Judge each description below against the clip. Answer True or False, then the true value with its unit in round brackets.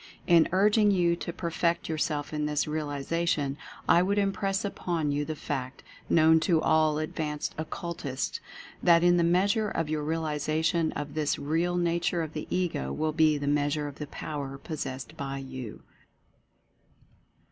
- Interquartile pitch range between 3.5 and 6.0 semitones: False (2.6 semitones)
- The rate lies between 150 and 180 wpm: True (160 wpm)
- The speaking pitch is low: False (155 Hz)